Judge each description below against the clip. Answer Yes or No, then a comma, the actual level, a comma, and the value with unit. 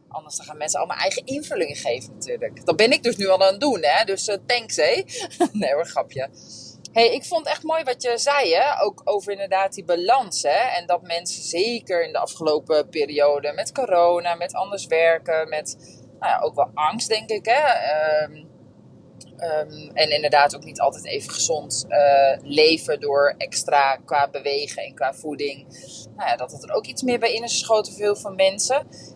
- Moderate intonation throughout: No, wide, 8.0 semitones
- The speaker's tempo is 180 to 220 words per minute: Yes, fast, 200 wpm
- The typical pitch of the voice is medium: Yes, medium, 175 Hz